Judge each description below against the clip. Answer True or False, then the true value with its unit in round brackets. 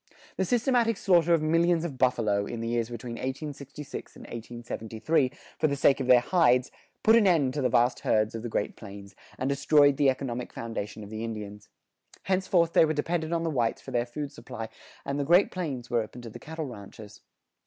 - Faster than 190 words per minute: True (205 wpm)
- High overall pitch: False (130 Hz)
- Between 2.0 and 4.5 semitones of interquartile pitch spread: False (5.6 semitones)